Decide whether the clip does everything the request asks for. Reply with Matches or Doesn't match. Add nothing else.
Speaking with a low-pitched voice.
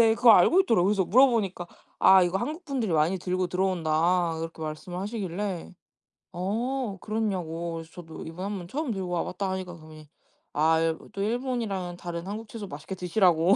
Doesn't match